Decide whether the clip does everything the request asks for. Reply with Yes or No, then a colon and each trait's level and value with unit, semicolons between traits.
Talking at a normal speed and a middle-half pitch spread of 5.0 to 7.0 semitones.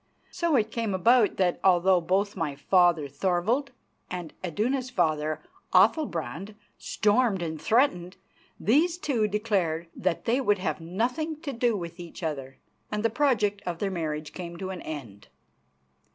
Yes: average, 150 wpm; wide, 5.4 semitones